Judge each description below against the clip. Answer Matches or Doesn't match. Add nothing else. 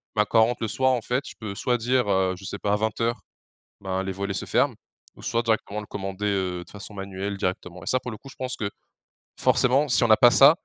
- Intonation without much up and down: Doesn't match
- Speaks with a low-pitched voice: Matches